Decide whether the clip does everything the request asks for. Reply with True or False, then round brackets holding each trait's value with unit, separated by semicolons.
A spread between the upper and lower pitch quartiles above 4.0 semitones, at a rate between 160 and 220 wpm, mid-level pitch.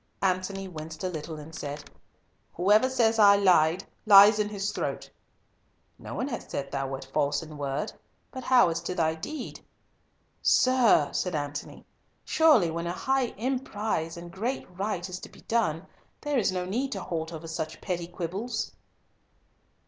True (5.2 semitones; 165 wpm; 180 Hz)